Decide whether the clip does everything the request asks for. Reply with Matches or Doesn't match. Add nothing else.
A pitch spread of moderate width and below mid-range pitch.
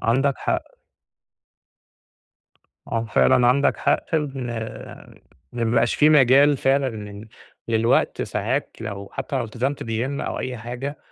Matches